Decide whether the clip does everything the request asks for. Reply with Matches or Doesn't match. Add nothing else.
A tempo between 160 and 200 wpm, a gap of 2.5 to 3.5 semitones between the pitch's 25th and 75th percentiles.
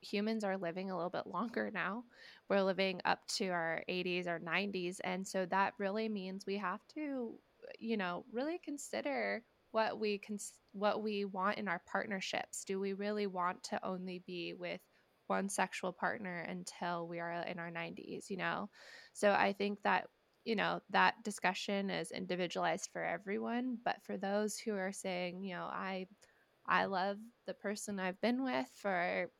Matches